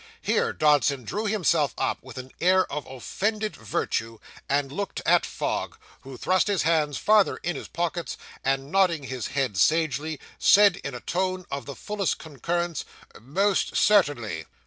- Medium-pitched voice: Yes, medium, 155 Hz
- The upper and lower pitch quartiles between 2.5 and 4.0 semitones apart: No, wide, 5.6 semitones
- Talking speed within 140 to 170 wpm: Yes, average, 155 wpm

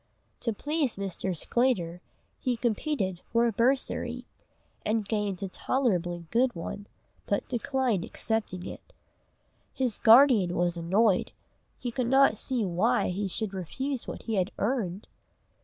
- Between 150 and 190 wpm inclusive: No, slow, 135 wpm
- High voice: Yes, high, 220 Hz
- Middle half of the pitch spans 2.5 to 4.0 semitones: No, average, 5.0 semitones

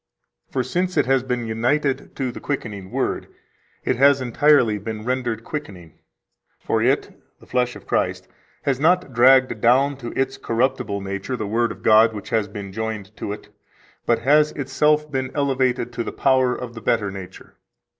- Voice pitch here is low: Yes, low, 125 Hz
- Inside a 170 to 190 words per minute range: Yes, average, 175 wpm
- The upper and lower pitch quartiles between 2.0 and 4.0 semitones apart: Yes, average, 3.5 semitones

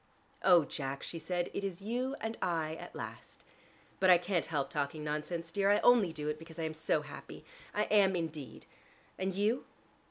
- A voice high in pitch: No, medium, 170 Hz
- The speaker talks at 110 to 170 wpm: No, average, 185 wpm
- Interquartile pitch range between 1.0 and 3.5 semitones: No, average, 4.2 semitones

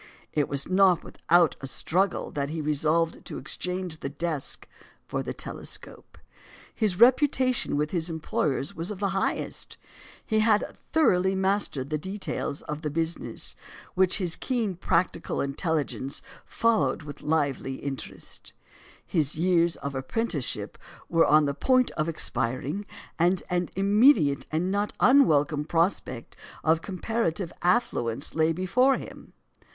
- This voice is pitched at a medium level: Yes, medium, 165 Hz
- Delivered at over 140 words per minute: No, slow, 135 wpm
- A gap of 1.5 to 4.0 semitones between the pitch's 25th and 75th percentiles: No, average, 4.5 semitones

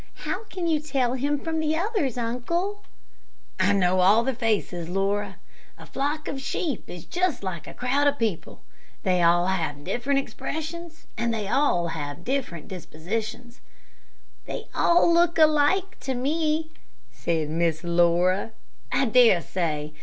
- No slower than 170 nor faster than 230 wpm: No, average, 140 wpm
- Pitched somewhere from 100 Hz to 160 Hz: No, high, 240 Hz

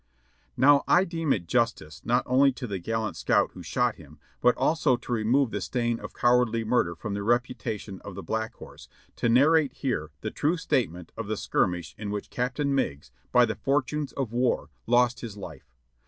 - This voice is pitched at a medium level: No, low, 120 Hz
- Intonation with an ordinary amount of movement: Yes, average, 4.4 semitones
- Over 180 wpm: Yes, average, 190 wpm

